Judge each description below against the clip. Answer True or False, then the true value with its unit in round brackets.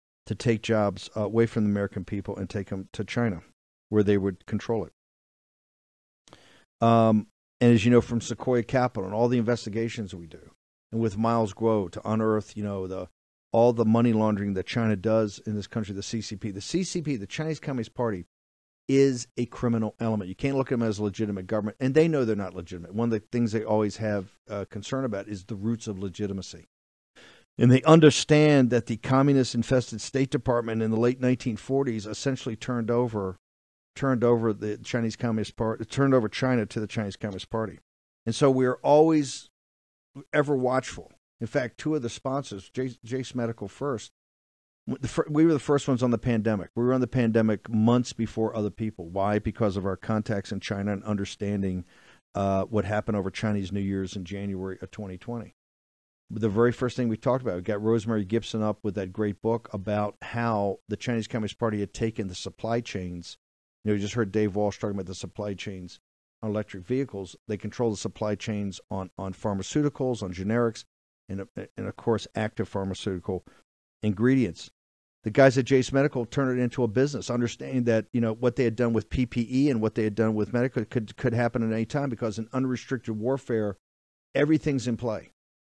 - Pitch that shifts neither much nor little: True (3.2 semitones)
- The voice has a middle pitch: False (110 Hz)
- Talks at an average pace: True (190 wpm)